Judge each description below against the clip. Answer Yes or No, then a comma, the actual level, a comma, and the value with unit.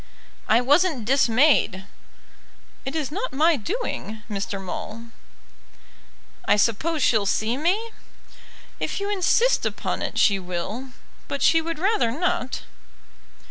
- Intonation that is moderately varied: No, wide, 7.4 semitones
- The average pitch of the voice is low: No, very high, 270 Hz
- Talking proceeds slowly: Yes, slow, 120 wpm